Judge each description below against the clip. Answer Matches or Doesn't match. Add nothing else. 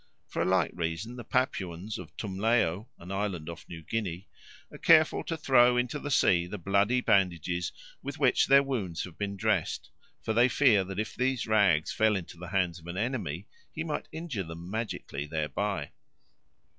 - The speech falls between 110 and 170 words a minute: Doesn't match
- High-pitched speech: Doesn't match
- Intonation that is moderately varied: Doesn't match